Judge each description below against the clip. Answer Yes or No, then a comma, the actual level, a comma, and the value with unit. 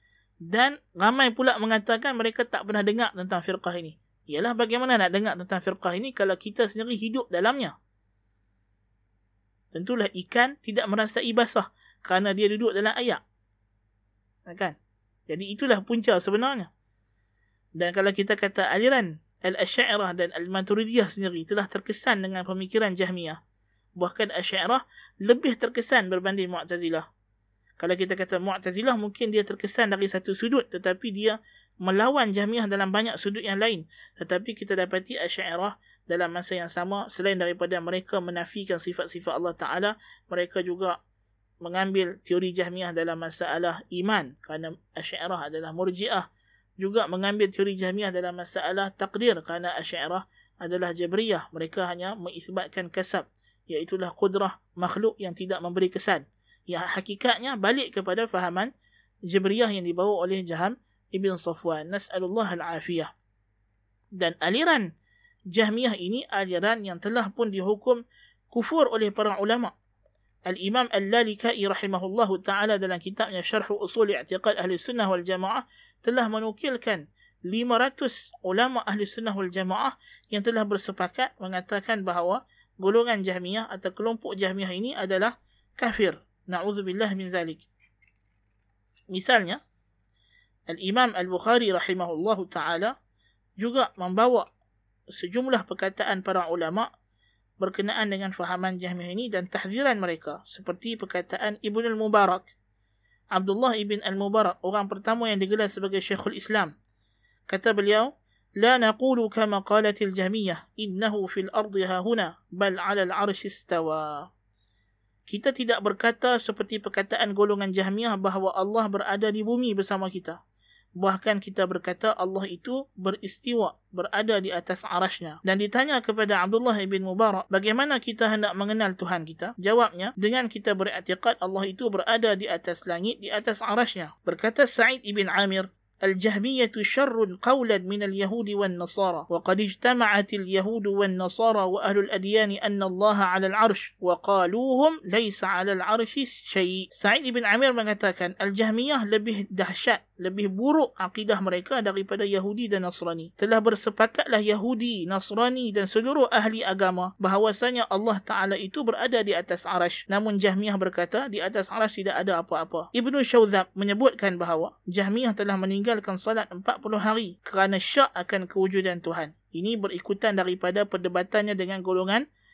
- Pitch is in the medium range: No, high, 195 Hz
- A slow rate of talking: No, average, 130 wpm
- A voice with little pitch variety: No, average, 3.6 semitones